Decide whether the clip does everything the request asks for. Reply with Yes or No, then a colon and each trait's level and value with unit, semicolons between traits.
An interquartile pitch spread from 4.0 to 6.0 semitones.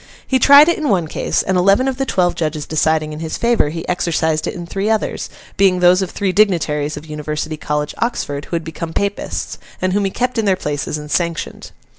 Yes: average, 4.5 semitones